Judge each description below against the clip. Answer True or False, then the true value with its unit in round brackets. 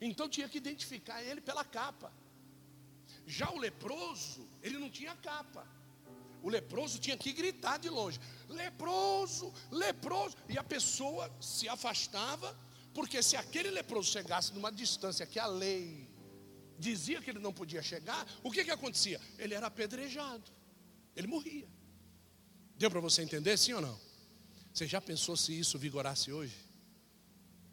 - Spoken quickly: False (145 wpm)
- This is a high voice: True (200 Hz)